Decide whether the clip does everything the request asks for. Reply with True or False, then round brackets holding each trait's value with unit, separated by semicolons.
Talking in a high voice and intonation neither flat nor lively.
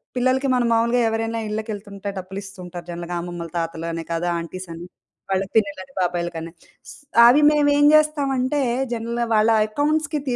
False (215 Hz; 6.4 semitones)